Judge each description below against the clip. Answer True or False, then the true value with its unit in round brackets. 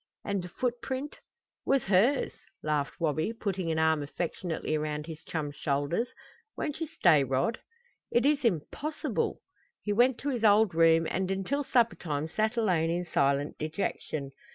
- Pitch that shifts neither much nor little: False (6.9 semitones)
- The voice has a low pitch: False (180 Hz)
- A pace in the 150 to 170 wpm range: True (155 wpm)